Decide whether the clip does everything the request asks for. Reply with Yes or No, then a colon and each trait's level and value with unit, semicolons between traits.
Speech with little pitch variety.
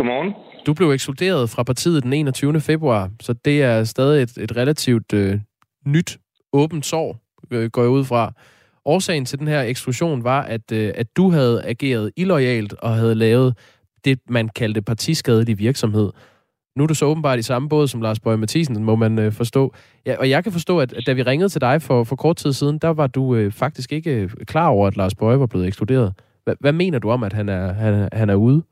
No: average, 4.6 semitones